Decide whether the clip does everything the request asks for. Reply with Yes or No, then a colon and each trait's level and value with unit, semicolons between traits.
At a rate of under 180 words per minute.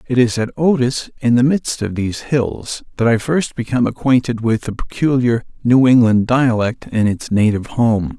No: average, 185 wpm